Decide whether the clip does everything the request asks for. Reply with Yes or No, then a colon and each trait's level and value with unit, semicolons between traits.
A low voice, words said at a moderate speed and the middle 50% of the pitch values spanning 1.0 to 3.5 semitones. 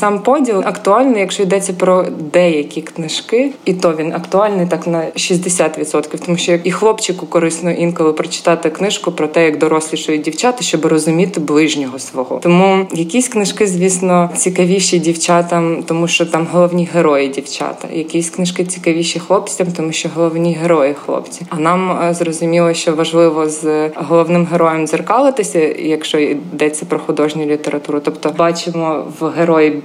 No: medium, 170 Hz; average, 145 wpm; narrow, 2.4 semitones